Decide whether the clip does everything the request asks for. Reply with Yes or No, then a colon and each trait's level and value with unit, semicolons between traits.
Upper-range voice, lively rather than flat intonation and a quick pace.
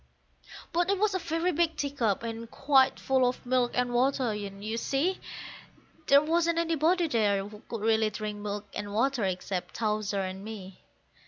No: high, 240 Hz; wide, 6.3 semitones; average, 170 wpm